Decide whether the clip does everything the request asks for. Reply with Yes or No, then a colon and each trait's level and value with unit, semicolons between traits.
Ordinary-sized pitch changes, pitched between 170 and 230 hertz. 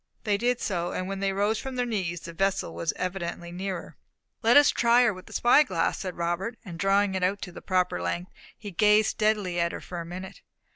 Yes: average, 3.4 semitones; high, 190 Hz